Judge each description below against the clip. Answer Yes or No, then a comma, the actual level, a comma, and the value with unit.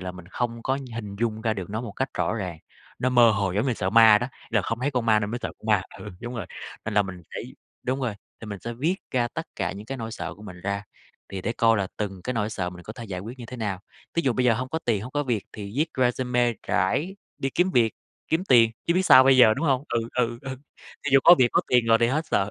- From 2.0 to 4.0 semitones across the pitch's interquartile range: Yes, average, 3.7 semitones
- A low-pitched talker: Yes, low, 115 Hz